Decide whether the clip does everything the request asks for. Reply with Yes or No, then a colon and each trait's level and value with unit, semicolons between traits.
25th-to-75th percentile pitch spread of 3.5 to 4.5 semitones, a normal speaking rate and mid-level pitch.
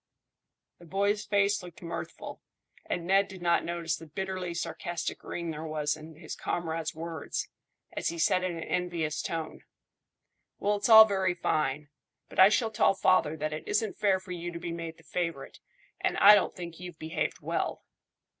No: average, 2.9 semitones; average, 180 wpm; medium, 170 Hz